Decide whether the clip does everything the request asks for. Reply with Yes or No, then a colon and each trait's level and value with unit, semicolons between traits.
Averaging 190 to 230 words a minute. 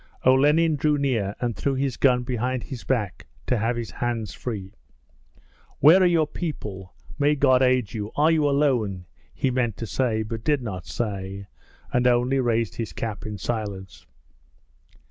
No: average, 165 wpm